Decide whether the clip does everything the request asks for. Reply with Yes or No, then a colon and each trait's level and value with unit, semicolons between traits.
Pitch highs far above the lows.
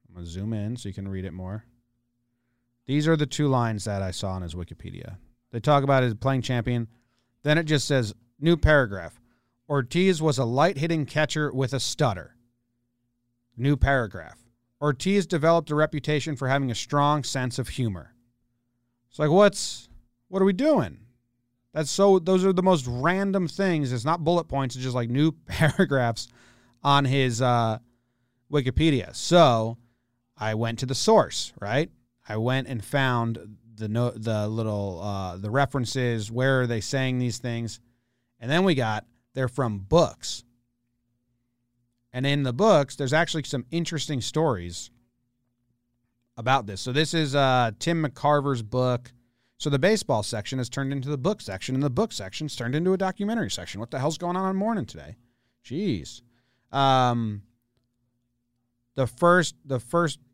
No: average, 3.6 semitones